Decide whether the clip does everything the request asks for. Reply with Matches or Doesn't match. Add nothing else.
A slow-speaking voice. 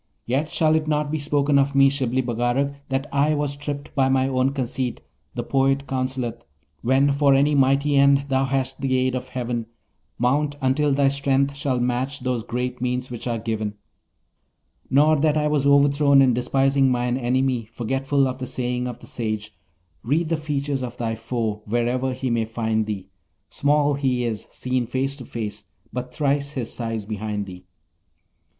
Doesn't match